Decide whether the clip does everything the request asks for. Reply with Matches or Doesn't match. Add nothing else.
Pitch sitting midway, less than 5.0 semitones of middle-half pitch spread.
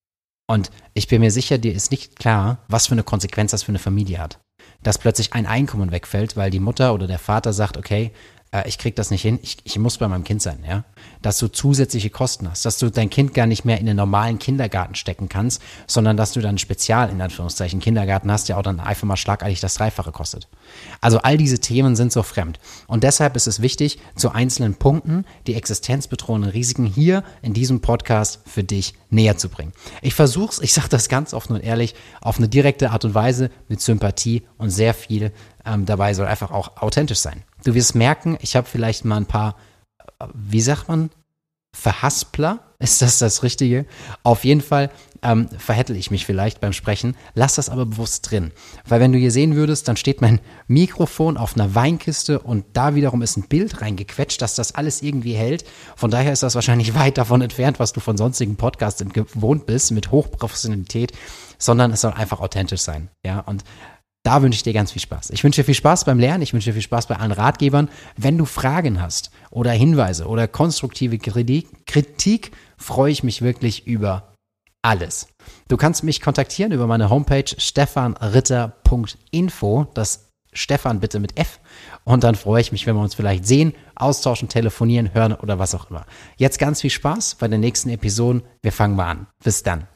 Doesn't match